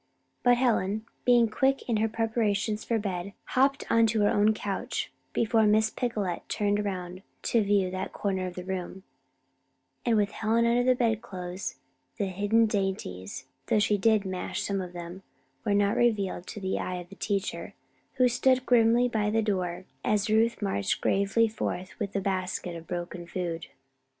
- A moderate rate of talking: Yes, average, 170 wpm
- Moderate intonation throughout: Yes, average, 3.2 semitones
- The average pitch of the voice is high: Yes, high, 205 Hz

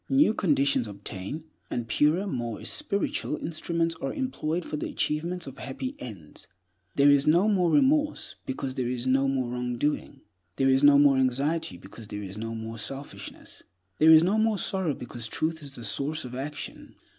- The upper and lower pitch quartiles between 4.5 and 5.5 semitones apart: Yes, average, 5.2 semitones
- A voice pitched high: No, medium, 140 Hz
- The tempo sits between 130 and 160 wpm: No, average, 180 wpm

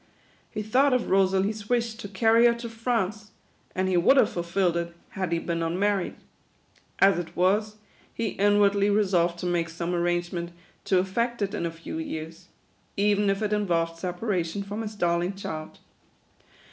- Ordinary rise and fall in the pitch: Yes, average, 3.5 semitones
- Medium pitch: No, high, 195 Hz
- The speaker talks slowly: No, average, 175 wpm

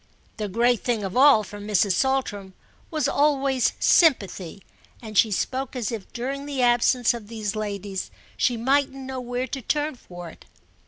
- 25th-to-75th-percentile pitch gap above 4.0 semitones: Yes, average, 4.4 semitones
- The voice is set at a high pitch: Yes, high, 240 Hz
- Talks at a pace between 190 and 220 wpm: No, average, 165 wpm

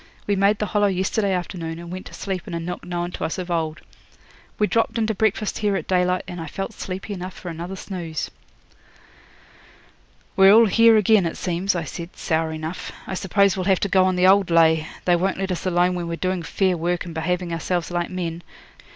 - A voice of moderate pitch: Yes, medium, 180 Hz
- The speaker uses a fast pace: Yes, fast, 220 wpm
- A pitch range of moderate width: No, narrow, 2.2 semitones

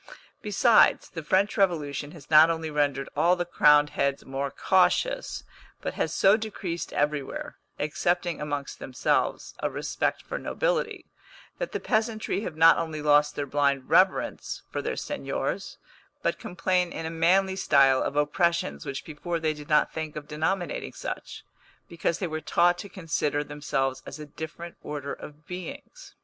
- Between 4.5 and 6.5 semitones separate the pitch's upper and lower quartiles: No, average, 3.5 semitones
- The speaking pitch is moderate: Yes, medium, 160 Hz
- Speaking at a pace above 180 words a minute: No, average, 160 wpm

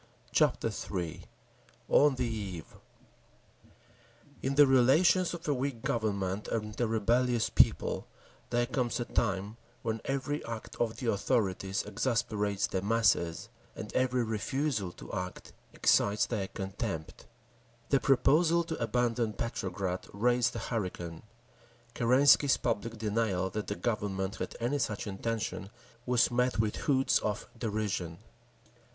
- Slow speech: Yes, slow, 125 wpm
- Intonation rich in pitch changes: No, average, 3.8 semitones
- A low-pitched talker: Yes, low, 115 Hz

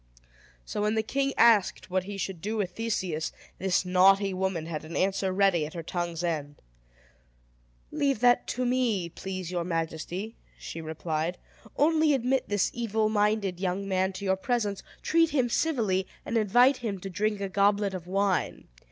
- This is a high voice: Yes, high, 195 Hz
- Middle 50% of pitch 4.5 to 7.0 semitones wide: No, average, 3.7 semitones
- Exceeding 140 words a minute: Yes, average, 170 wpm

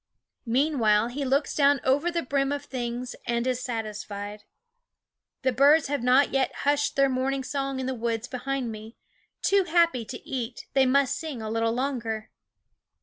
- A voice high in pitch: Yes, very high, 260 Hz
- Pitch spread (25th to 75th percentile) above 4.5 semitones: No, average, 3.1 semitones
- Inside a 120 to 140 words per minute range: No, average, 165 wpm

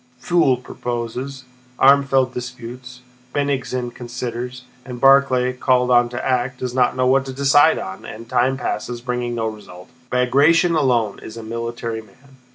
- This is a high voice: No, low, 125 Hz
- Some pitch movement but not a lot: No, narrow, 1.7 semitones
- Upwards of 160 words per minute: No, average, 150 wpm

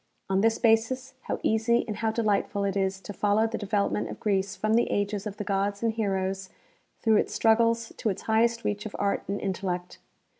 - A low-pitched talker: No, high, 210 Hz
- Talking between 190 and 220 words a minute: Yes, average, 200 wpm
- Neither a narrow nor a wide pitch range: No, narrow, 2.2 semitones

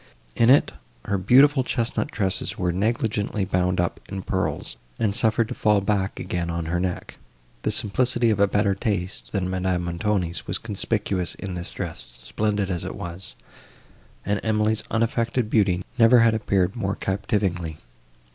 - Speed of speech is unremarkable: Yes, average, 155 wpm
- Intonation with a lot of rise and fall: No, average, 3.3 semitones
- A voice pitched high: No, low, 100 Hz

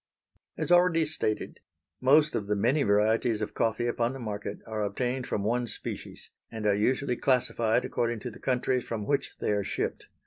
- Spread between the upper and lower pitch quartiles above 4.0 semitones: No, average, 3.4 semitones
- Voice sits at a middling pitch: No, low, 120 Hz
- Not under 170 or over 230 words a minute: Yes, average, 180 wpm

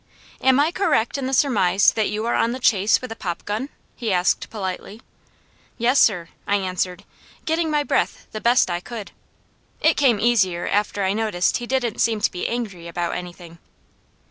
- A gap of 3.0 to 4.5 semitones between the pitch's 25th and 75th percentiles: No, average, 4.9 semitones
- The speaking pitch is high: Yes, high, 215 Hz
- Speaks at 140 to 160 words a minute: No, average, 180 wpm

